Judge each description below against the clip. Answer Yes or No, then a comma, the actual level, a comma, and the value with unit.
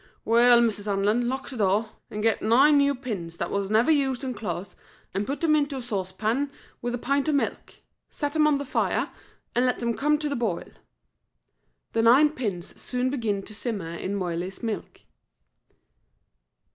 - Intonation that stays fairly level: No, average, 5.3 semitones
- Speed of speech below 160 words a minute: No, average, 180 wpm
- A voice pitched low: No, high, 235 Hz